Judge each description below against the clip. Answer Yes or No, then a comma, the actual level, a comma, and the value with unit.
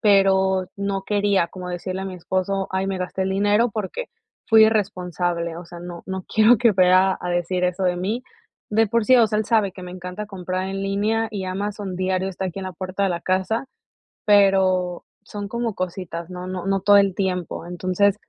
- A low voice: No, high, 190 Hz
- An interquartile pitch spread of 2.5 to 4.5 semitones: No, narrow, 2.0 semitones